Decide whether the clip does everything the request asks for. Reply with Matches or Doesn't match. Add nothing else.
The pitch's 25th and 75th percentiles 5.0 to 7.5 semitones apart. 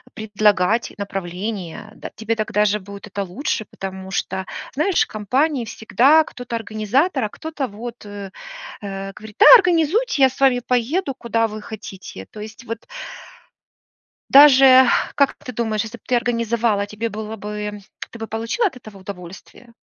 Doesn't match